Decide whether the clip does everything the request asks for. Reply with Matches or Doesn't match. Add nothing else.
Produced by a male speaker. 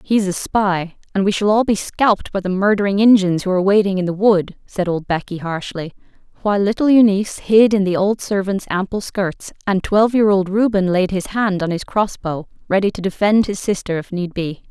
Doesn't match